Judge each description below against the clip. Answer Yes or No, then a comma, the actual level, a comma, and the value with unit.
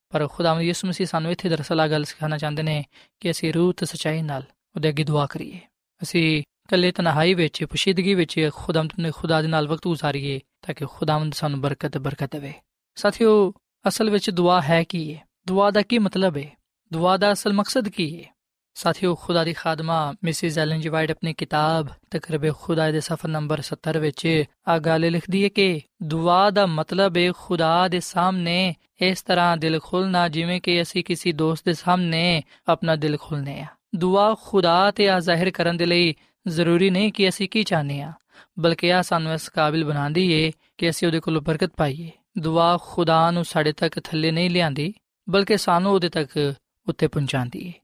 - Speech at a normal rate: No, fast, 185 wpm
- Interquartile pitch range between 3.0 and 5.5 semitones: No, narrow, 2.6 semitones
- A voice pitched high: No, medium, 170 Hz